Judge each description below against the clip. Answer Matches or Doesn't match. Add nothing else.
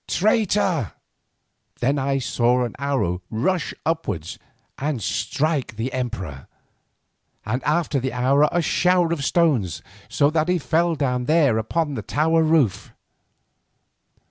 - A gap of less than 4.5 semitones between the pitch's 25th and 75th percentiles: Doesn't match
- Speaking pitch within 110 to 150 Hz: Matches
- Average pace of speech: Doesn't match